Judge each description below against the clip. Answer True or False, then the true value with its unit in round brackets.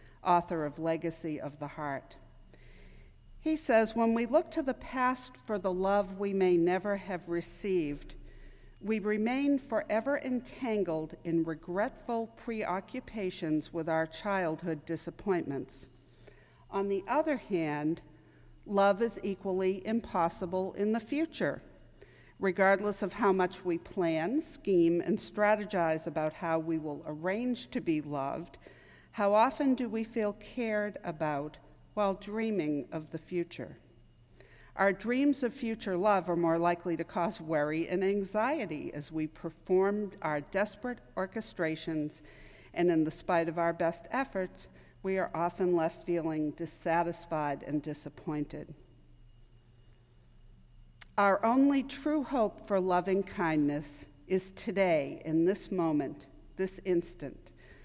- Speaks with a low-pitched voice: False (180 Hz)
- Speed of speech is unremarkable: False (125 wpm)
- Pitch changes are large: False (4.6 semitones)